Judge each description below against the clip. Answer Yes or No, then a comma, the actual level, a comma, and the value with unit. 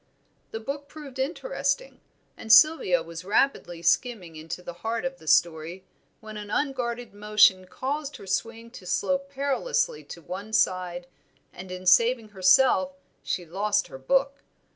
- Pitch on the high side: Yes, high, 215 Hz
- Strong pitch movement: Yes, wide, 6.6 semitones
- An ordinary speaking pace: Yes, average, 145 wpm